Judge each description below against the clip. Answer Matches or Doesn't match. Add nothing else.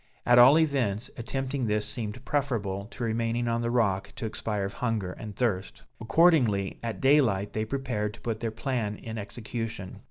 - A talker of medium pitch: Doesn't match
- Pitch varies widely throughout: Doesn't match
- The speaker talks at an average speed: Matches